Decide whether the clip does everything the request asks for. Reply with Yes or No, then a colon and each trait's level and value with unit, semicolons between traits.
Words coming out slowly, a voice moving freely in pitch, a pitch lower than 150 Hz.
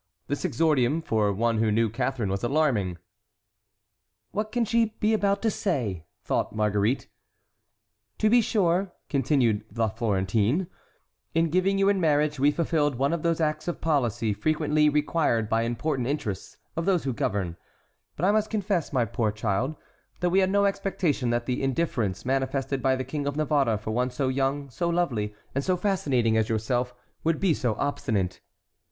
No: average, 170 wpm; wide, 6.8 semitones; medium, 140 Hz